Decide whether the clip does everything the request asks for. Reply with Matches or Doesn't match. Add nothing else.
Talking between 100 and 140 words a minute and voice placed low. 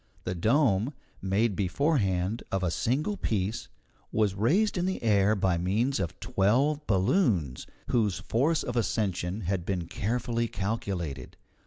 Matches